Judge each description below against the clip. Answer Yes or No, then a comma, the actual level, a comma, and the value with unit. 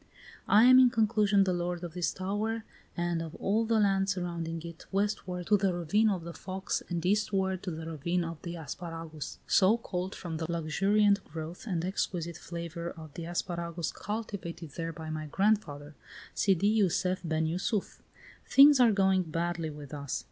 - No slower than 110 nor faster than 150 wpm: No, average, 170 wpm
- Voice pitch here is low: No, medium, 180 Hz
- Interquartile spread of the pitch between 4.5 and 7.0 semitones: No, average, 3.3 semitones